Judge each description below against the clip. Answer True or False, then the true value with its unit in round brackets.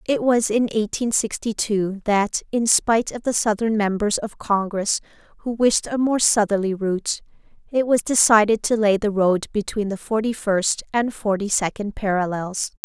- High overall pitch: True (210 Hz)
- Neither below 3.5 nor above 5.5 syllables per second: True (4.7 syllables/s)